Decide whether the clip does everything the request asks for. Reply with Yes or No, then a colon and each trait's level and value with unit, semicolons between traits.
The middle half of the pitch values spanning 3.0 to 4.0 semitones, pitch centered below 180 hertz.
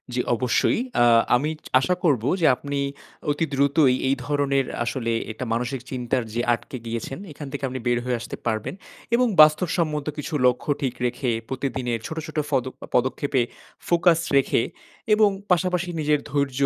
Yes: average, 3.5 semitones; low, 135 Hz